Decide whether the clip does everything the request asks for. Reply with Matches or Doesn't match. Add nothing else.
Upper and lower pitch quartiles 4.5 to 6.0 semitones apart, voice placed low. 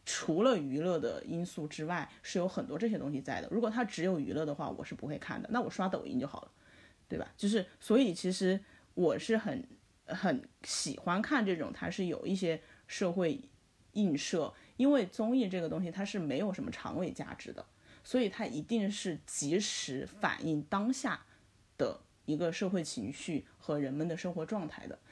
Doesn't match